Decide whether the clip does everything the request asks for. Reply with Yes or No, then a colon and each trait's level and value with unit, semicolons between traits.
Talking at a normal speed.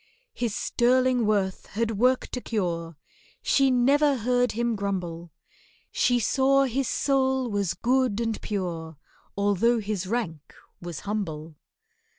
No: slow, 125 wpm